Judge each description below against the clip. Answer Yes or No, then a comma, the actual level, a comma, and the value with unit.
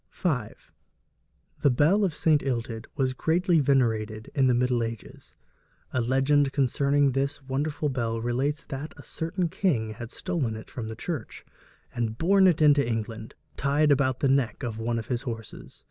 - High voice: No, low, 135 Hz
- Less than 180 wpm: Yes, average, 165 wpm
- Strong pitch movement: No, average, 4.1 semitones